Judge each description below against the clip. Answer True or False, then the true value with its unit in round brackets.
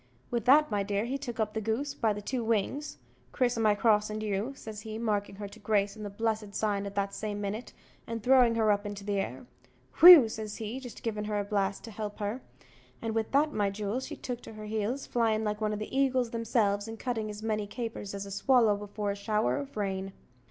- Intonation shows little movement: True (2.1 semitones)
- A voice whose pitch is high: True (215 Hz)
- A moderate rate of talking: False (235 wpm)